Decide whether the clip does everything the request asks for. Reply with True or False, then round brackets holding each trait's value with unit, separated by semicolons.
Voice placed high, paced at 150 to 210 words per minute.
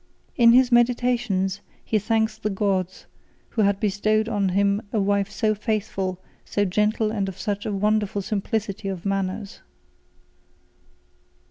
False (205 Hz; 135 wpm)